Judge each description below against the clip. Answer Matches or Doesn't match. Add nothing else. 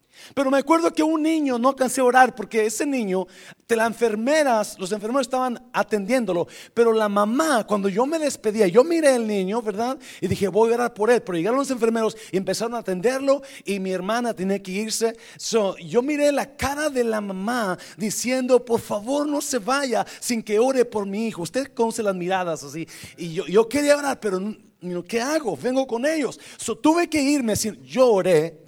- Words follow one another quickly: Matches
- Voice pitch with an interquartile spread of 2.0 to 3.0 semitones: Doesn't match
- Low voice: Doesn't match